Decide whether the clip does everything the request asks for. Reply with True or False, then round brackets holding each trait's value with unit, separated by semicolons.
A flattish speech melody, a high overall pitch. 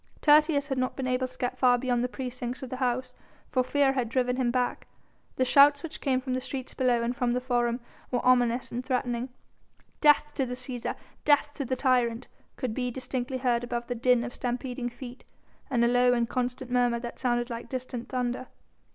True (1.1 semitones; 250 Hz)